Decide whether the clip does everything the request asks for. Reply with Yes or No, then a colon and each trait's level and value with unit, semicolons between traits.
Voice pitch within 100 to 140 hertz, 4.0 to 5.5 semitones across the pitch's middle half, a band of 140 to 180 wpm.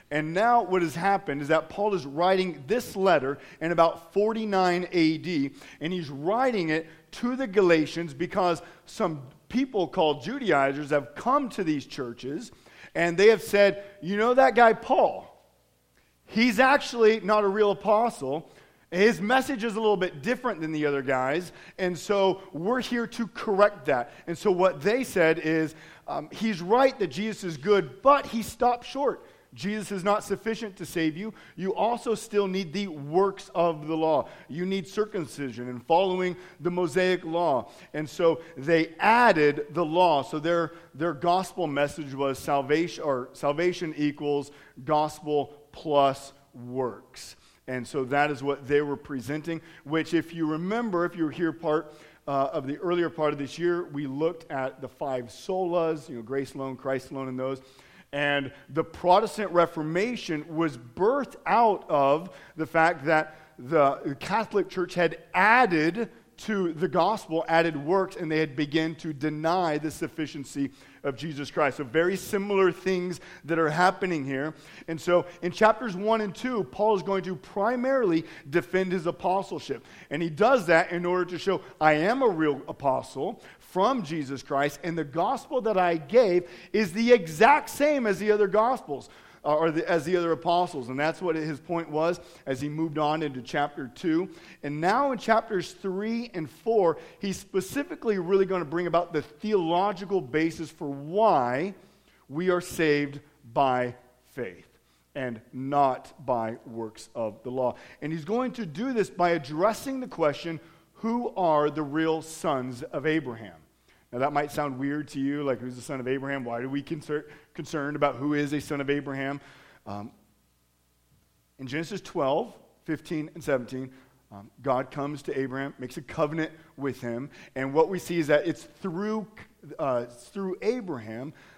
No: medium, 165 Hz; average, 5.0 semitones; average, 170 wpm